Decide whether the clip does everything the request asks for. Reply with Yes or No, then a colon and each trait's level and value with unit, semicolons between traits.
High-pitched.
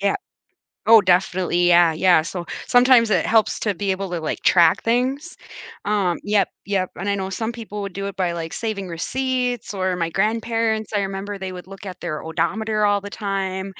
Yes: high, 195 Hz